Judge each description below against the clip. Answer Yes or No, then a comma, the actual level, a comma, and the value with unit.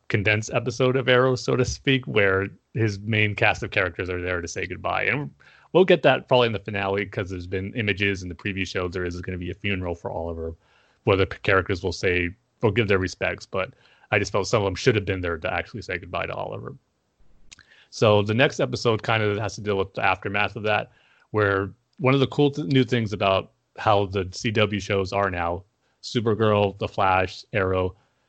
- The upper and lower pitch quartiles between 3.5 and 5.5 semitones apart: Yes, average, 4.0 semitones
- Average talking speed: No, fast, 215 wpm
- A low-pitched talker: Yes, low, 100 Hz